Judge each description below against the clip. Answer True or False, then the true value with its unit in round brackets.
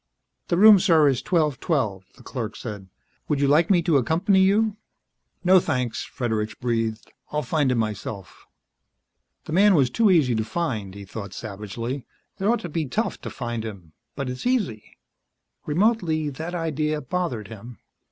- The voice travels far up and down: True (7.4 semitones)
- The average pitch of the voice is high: False (140 Hz)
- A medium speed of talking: True (165 wpm)